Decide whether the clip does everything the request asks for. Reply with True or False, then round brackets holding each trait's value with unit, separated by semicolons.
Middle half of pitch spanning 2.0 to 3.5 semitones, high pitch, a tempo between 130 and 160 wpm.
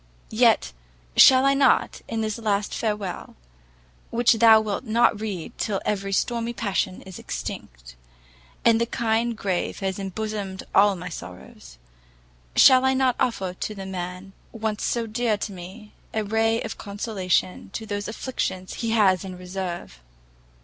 True (3.2 semitones; 210 Hz; 150 wpm)